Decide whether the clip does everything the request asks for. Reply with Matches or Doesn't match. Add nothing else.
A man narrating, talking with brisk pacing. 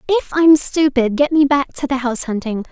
Doesn't match